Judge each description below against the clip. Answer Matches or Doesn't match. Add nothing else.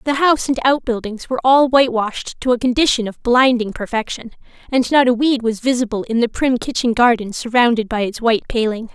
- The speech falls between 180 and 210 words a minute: Matches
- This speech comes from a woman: Matches